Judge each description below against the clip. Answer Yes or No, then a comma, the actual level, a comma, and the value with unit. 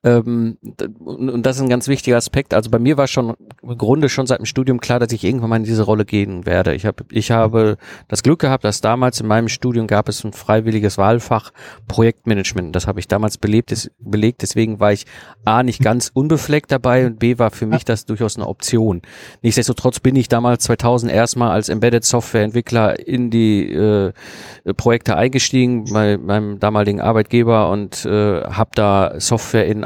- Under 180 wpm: No, average, 185 wpm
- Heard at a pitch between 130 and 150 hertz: No, low, 115 Hz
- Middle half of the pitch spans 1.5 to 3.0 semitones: Yes, narrow, 2.6 semitones